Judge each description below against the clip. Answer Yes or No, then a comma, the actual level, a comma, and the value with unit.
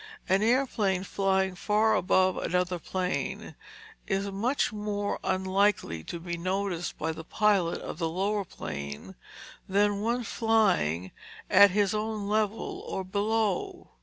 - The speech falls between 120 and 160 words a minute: Yes, slow, 135 wpm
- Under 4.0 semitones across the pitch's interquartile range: Yes, narrow, 2.6 semitones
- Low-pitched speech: No, high, 195 Hz